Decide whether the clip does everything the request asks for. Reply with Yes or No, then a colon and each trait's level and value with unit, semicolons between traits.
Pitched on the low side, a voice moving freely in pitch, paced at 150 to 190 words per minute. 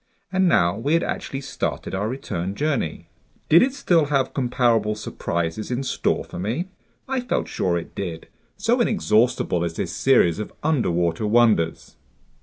Yes: low, 120 Hz; wide, 8.9 semitones; average, 155 wpm